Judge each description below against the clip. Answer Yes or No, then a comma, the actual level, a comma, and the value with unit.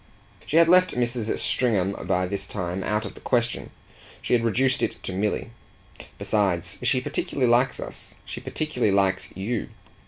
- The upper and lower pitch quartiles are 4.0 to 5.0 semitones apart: Yes, average, 4.4 semitones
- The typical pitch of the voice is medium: No, low, 115 Hz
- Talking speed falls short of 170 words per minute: Yes, average, 160 wpm